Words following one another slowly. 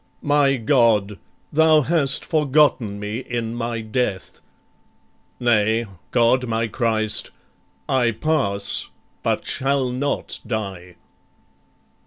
Yes: slow, 95 wpm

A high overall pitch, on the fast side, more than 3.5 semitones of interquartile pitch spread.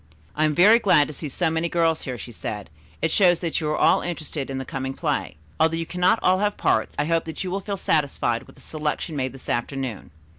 No: medium, 160 Hz; fast, 245 wpm; average, 4.5 semitones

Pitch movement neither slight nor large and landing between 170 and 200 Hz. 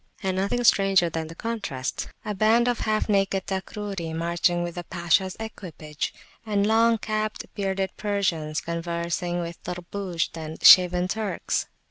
Yes: average, 3.5 semitones; high, 190 Hz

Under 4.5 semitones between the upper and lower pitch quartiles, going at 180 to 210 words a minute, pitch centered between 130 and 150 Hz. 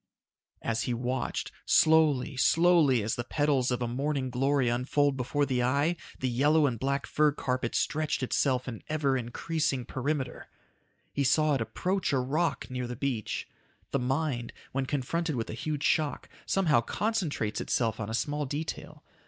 No: average, 3.4 semitones; average, 160 wpm; low, 135 Hz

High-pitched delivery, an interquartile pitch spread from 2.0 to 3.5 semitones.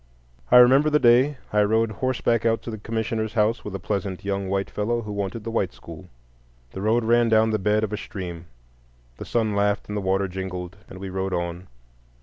No: low, 105 Hz; average, 3.0 semitones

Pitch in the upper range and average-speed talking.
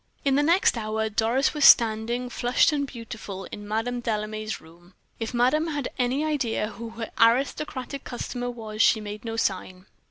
Yes: high, 230 Hz; average, 165 wpm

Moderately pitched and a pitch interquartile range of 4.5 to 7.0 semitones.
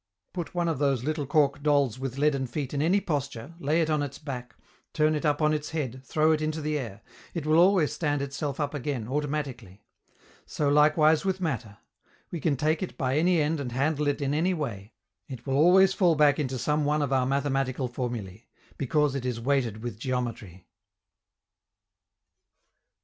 No: medium, 145 Hz; average, 3.0 semitones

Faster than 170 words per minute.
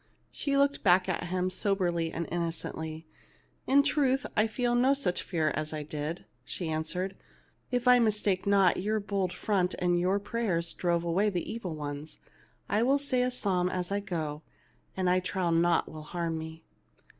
Yes: average, 180 wpm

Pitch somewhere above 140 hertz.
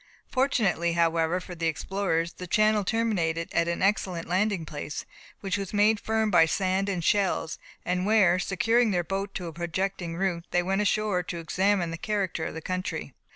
Yes: medium, 185 Hz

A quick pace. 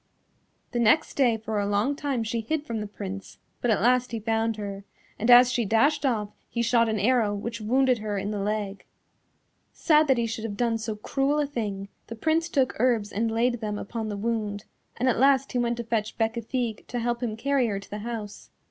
Yes: fast, 220 wpm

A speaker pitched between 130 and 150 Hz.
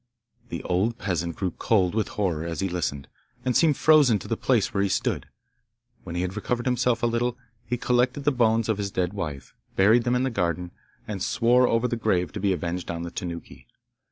No: low, 105 Hz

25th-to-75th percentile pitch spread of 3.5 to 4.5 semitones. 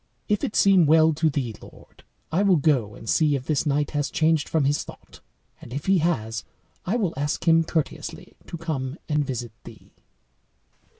No: average, 3.1 semitones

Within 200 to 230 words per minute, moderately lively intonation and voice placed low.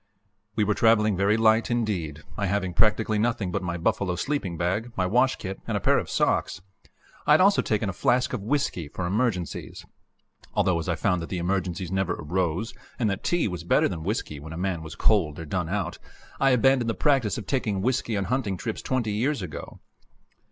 Yes: fast, 205 wpm; average, 4.4 semitones; low, 100 Hz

